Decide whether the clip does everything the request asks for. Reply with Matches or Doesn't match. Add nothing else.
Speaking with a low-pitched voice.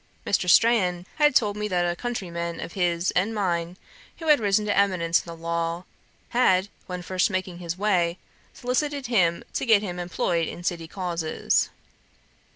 Doesn't match